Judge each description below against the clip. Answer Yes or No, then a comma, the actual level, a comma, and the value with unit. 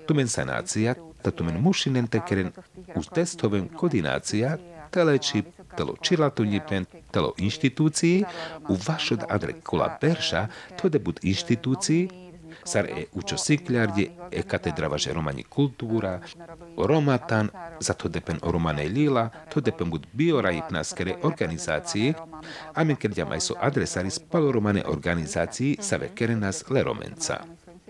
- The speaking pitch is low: Yes, low, 130 Hz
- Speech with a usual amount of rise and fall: No, wide, 8.1 semitones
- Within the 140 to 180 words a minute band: No, average, 125 wpm